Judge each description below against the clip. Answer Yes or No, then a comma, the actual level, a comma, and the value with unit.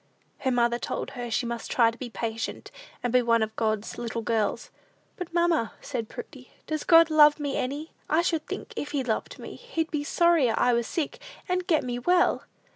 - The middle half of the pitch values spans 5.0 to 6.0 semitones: Yes, wide, 5.6 semitones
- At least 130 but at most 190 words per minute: No, average, 200 wpm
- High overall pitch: Yes, very high, 260 Hz